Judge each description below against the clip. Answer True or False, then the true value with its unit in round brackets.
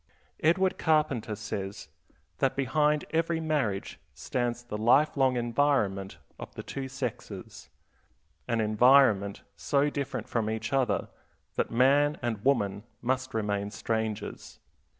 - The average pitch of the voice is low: True (125 Hz)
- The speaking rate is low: True (120 wpm)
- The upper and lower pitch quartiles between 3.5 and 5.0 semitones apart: True (4.7 semitones)